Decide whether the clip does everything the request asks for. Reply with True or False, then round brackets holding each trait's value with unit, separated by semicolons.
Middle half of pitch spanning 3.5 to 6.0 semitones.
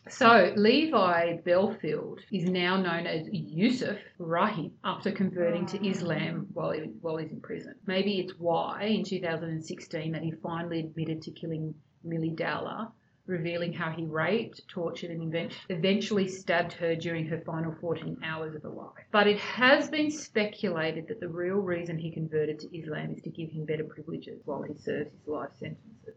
False (3.1 semitones)